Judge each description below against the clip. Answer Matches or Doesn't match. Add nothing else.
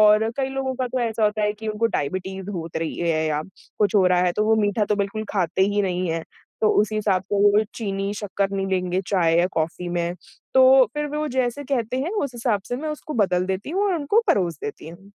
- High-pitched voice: Matches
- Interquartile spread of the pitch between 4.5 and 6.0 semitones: Matches